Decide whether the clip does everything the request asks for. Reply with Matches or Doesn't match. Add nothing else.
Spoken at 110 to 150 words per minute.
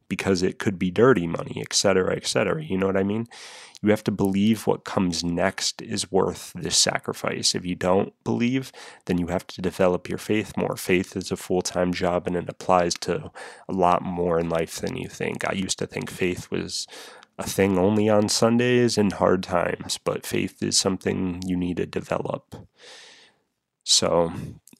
Doesn't match